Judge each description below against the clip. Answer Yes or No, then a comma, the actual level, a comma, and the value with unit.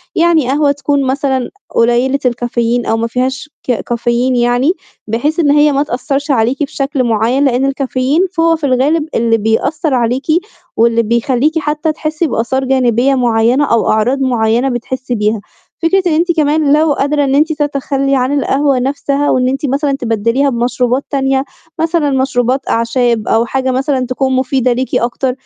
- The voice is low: No, very high, 265 Hz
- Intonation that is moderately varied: Yes, average, 3.0 semitones